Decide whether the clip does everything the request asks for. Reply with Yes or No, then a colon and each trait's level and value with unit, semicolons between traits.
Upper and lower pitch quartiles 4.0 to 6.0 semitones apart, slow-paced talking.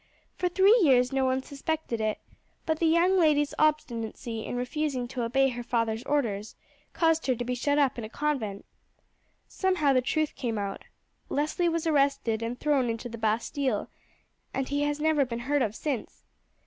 No: average, 4.4 semitones; average, 175 wpm